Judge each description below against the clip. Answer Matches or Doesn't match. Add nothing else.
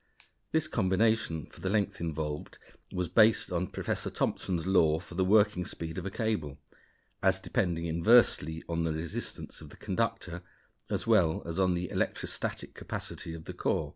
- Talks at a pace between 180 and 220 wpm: Doesn't match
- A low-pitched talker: Matches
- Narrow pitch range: Doesn't match